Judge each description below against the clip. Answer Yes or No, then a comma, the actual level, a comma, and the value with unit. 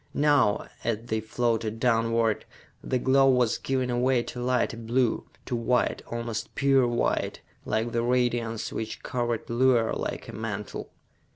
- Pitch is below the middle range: Yes, low, 120 Hz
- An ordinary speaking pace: Yes, average, 145 wpm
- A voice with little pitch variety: Yes, narrow, 1.8 semitones